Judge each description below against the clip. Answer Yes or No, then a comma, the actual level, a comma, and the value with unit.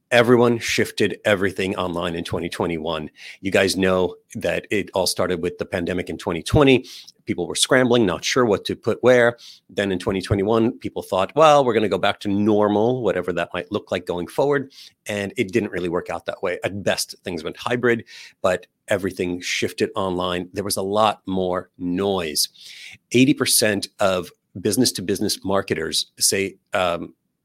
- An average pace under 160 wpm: No, average, 170 wpm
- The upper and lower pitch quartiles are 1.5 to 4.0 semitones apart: No, average, 4.6 semitones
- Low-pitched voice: Yes, low, 100 Hz